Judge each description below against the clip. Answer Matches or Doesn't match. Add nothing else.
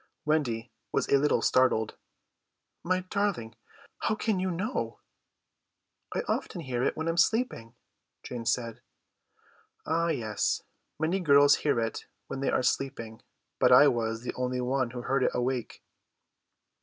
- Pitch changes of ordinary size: Doesn't match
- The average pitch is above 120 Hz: Matches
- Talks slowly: Doesn't match